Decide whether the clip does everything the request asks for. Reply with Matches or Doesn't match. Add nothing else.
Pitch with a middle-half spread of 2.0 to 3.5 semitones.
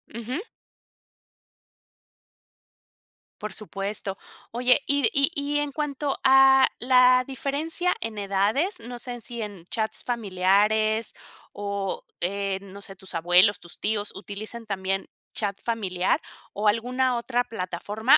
Doesn't match